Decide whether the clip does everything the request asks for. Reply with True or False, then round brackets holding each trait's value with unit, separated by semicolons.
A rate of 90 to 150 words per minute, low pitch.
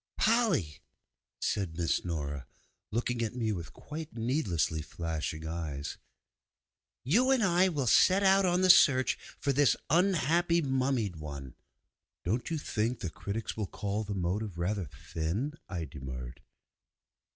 True (135 wpm; 110 Hz)